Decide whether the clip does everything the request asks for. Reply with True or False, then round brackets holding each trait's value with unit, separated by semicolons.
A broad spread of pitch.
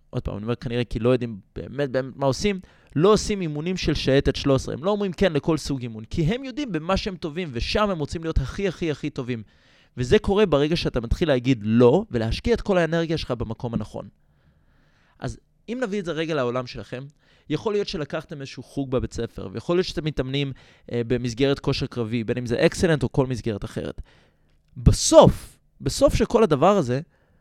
True (6.2 semitones)